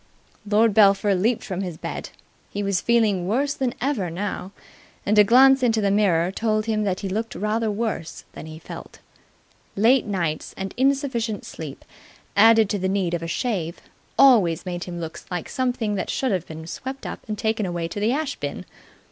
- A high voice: Yes, high, 205 Hz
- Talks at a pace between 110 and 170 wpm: No, average, 190 wpm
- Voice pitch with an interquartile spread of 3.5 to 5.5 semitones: Yes, average, 4.1 semitones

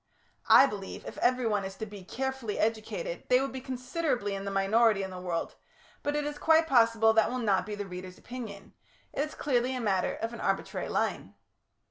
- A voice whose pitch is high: Yes, high, 225 Hz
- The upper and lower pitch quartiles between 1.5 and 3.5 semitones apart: No, average, 4.8 semitones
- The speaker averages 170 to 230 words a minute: Yes, average, 200 wpm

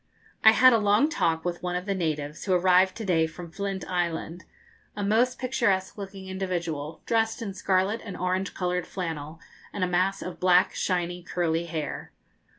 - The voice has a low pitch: No, medium, 185 Hz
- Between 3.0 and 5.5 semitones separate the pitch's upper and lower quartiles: No, narrow, 2.6 semitones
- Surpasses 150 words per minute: Yes, average, 175 wpm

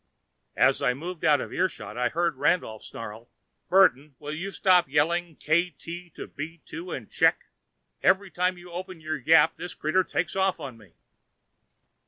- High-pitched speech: No, medium, 165 Hz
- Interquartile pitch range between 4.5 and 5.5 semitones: No, average, 3.7 semitones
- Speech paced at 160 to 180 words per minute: Yes, average, 165 wpm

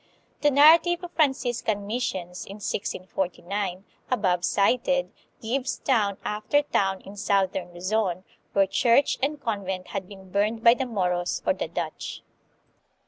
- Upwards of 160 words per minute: No, slow, 135 wpm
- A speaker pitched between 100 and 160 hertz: No, high, 205 Hz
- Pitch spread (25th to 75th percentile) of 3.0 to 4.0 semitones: No, average, 5.0 semitones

